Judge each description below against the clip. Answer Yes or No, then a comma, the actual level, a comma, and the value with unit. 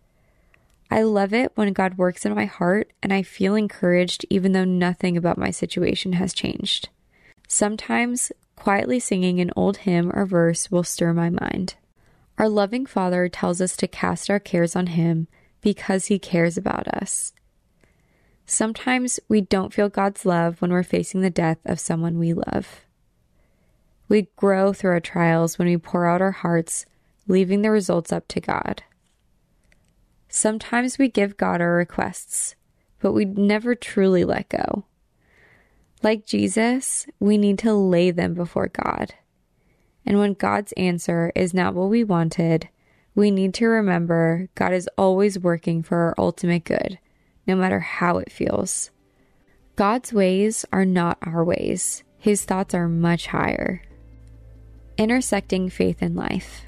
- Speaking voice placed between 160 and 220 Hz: Yes, high, 190 Hz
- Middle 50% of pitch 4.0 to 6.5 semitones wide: No, average, 3.2 semitones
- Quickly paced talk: No, average, 150 wpm